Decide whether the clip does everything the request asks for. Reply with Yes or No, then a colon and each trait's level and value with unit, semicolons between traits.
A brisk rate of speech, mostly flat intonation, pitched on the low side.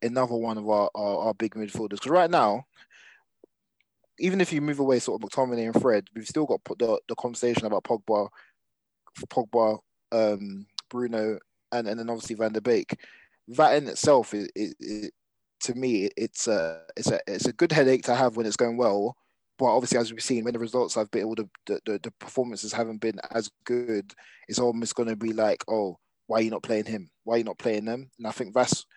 Yes: fast, 215 wpm; narrow, 2.3 semitones; low, 115 Hz